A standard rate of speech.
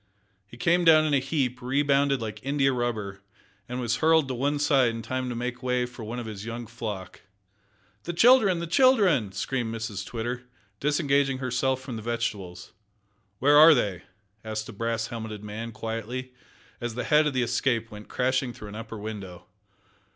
Yes: average, 180 wpm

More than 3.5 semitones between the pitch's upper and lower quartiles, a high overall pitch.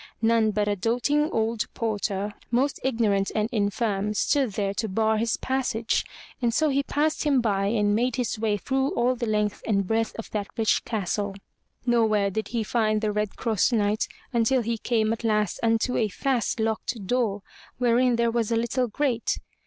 No: narrow, 2.4 semitones; high, 225 Hz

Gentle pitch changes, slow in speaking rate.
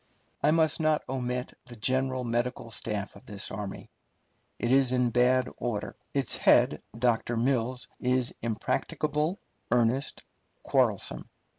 Yes: narrow, 2.1 semitones; slow, 125 wpm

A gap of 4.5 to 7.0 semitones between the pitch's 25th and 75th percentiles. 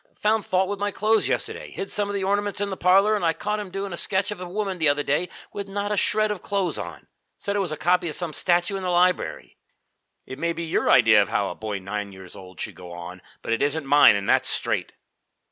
Yes: wide, 5.5 semitones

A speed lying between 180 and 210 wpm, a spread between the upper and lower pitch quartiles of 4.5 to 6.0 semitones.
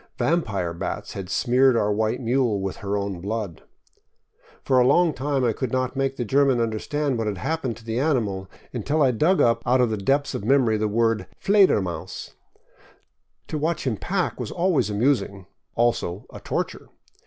Yes: average, 185 wpm; average, 4.8 semitones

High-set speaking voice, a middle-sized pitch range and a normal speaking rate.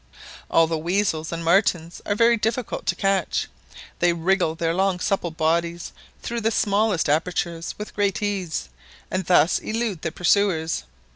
No: medium, 180 Hz; average, 3.6 semitones; average, 150 wpm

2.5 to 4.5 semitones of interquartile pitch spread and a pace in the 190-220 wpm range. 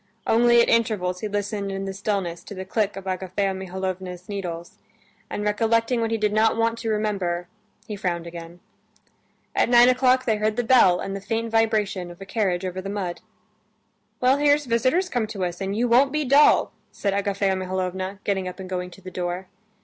Yes: average, 3.4 semitones; average, 195 wpm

